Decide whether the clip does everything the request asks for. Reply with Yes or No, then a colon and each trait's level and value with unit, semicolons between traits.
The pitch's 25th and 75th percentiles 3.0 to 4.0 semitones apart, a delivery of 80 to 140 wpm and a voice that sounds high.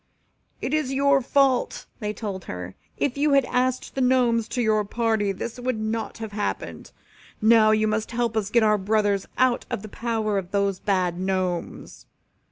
No: average, 3.5 semitones; average, 185 wpm; high, 220 Hz